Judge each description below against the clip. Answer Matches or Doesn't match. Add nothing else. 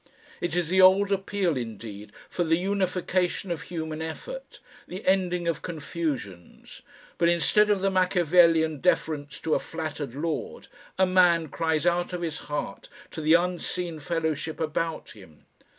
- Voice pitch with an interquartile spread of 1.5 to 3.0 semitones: Matches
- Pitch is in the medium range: Matches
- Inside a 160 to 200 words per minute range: Doesn't match